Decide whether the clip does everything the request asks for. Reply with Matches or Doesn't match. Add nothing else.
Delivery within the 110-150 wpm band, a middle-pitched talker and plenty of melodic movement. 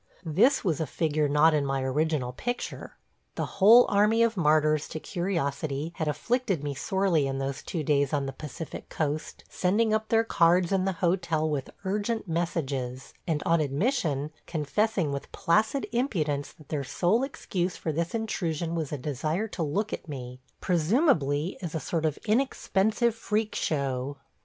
Doesn't match